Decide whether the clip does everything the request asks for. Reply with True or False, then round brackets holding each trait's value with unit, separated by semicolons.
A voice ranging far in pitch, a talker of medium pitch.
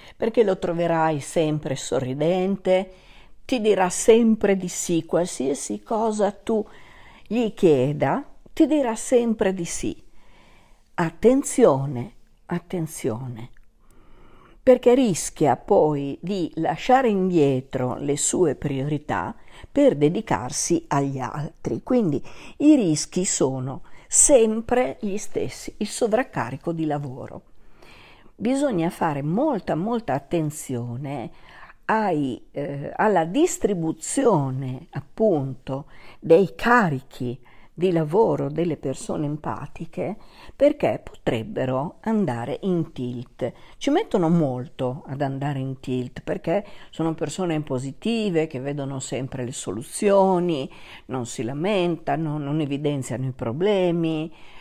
True (7.0 semitones; 160 Hz)